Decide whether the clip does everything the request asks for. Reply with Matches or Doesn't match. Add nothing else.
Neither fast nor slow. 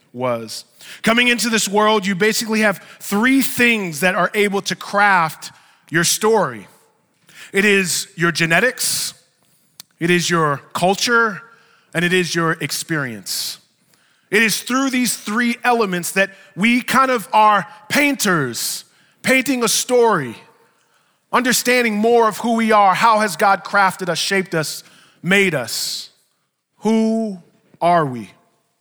Doesn't match